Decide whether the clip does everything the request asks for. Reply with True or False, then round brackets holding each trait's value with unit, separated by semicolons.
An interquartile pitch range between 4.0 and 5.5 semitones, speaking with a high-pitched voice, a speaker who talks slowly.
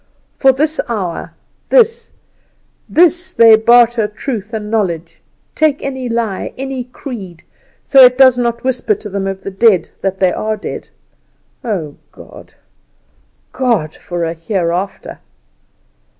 True (5.1 semitones; 225 Hz; 125 wpm)